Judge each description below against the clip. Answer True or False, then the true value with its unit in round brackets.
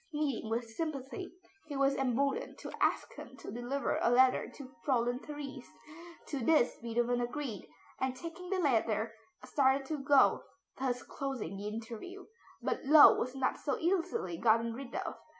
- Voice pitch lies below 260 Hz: False (265 Hz)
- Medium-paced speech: True (155 wpm)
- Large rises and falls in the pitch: False (3.5 semitones)